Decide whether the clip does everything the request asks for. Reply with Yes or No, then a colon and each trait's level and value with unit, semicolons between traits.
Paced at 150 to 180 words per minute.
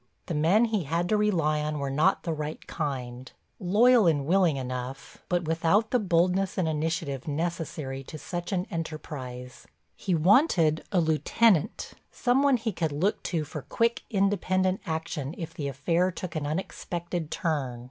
Yes: average, 160 wpm